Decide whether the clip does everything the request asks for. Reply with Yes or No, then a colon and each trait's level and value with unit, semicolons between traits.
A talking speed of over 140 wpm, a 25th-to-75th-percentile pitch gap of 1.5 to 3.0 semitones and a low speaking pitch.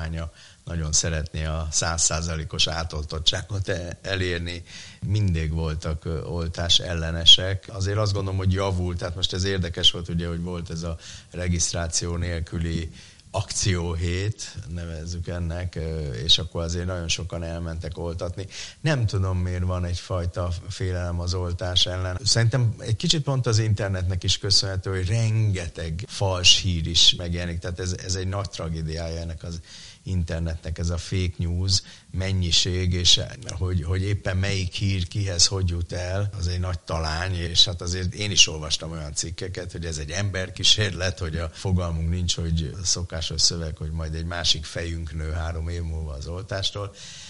Yes: average, 150 wpm; narrow, 2.4 semitones; very low, 90 Hz